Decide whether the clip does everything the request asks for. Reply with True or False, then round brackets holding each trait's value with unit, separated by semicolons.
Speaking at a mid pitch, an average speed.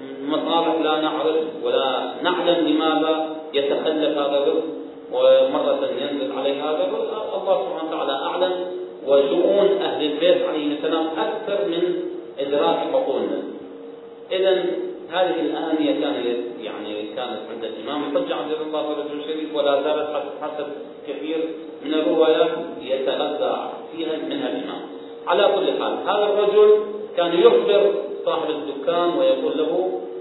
True (160 Hz; 125 wpm)